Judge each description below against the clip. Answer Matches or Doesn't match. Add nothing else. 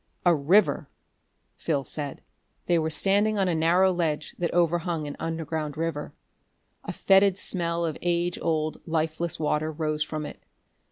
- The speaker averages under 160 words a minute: Matches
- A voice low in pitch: Doesn't match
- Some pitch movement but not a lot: Doesn't match